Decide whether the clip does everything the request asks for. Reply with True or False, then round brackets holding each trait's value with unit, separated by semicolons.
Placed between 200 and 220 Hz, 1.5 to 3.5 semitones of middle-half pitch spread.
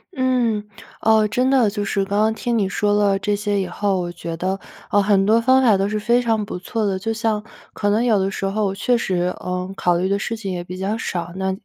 True (205 Hz; 2.5 semitones)